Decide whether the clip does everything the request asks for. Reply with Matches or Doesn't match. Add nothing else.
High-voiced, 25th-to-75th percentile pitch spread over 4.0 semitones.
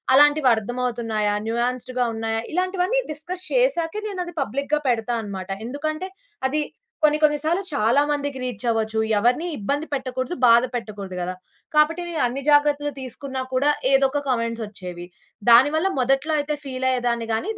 Matches